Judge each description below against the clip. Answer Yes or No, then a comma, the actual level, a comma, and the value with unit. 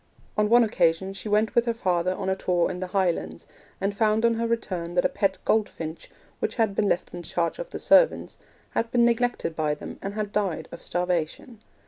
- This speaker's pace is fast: Yes, fast, 215 wpm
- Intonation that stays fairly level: No, average, 4.2 semitones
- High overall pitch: Yes, high, 195 Hz